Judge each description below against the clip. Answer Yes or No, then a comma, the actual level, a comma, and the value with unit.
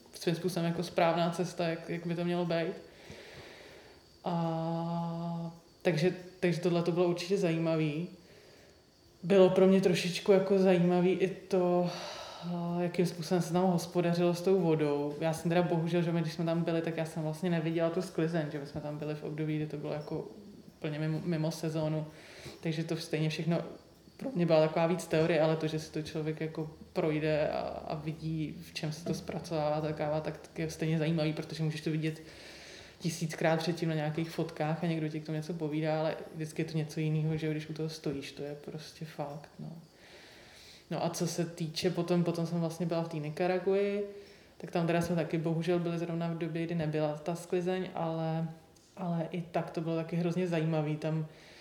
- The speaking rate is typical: No, fast, 195 wpm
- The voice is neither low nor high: Yes, medium, 165 Hz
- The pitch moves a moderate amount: No, narrow, 1.8 semitones